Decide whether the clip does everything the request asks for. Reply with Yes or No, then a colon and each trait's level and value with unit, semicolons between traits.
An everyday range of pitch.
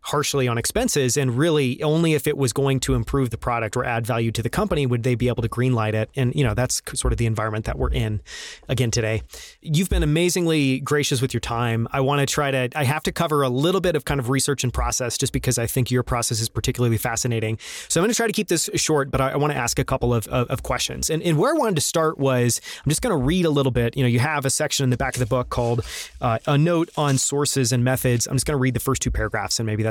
Yes: average, 3.5 semitones